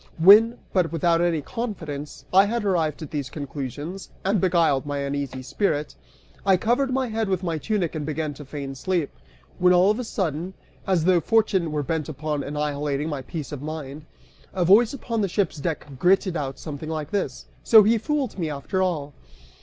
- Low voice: No, medium, 165 Hz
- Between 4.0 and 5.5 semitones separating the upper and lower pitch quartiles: Yes, average, 4.9 semitones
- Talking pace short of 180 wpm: No, average, 185 wpm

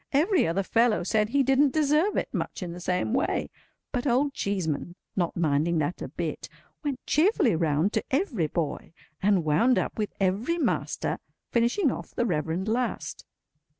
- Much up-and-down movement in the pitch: Yes, wide, 8.0 semitones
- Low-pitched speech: No, high, 215 Hz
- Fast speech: No, average, 160 wpm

